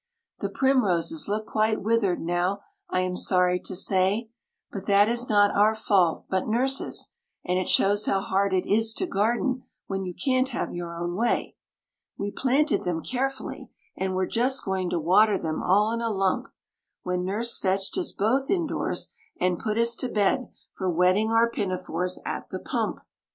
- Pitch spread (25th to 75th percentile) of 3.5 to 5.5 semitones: Yes, average, 4.0 semitones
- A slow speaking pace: No, average, 175 wpm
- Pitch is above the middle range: Yes, high, 200 Hz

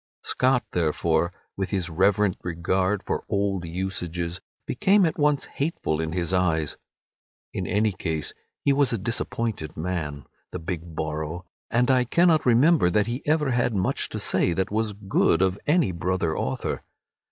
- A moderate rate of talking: Yes, average, 155 wpm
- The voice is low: Yes, very low, 95 Hz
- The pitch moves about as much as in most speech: No, wide, 5.8 semitones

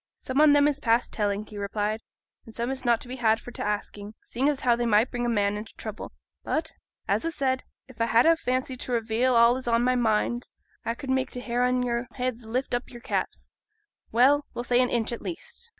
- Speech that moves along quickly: Yes, fast, 245 wpm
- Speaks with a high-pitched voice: Yes, high, 240 Hz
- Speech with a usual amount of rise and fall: No, narrow, 2.3 semitones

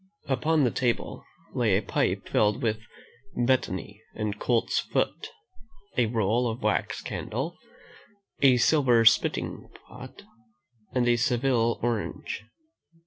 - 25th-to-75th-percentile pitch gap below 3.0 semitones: Yes, narrow, 2.5 semitones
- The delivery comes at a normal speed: No, slow, 115 wpm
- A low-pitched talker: Yes, low, 120 Hz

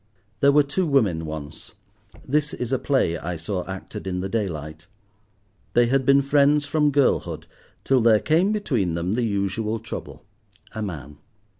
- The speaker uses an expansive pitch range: Yes, wide, 7.5 semitones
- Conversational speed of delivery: Yes, average, 155 wpm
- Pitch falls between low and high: No, low, 110 Hz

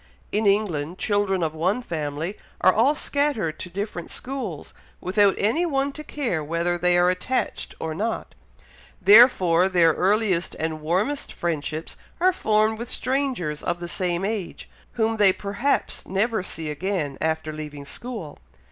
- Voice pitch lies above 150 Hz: Yes, high, 190 Hz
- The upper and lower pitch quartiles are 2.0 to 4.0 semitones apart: No, average, 5.1 semitones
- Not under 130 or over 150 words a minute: Yes, average, 145 wpm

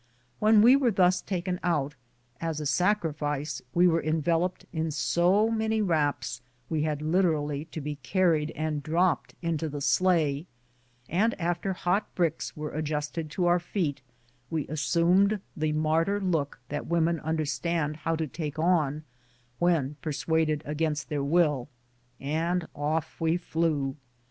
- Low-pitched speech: No, medium, 160 Hz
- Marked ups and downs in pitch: No, average, 2.9 semitones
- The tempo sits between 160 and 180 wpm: No, average, 140 wpm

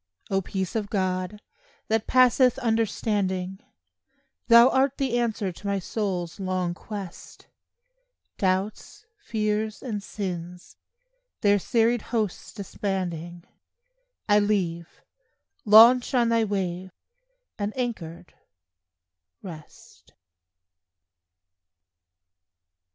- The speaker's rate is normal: No, slow, 85 wpm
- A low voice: No, high, 205 Hz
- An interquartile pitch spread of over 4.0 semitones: No, average, 3.5 semitones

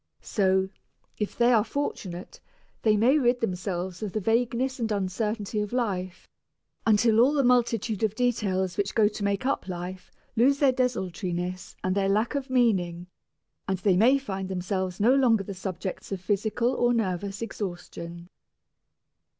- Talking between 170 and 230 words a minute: No, average, 155 wpm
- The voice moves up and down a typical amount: Yes, average, 4.1 semitones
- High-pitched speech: Yes, high, 210 Hz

